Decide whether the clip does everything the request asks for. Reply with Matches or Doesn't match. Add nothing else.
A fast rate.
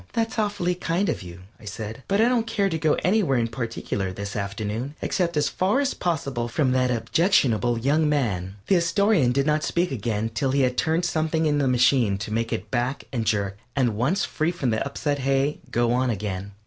Matches